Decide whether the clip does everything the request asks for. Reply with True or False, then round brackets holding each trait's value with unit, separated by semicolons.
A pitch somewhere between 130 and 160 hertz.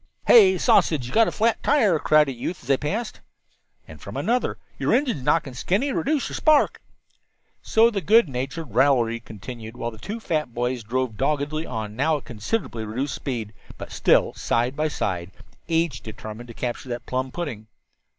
True (135 Hz)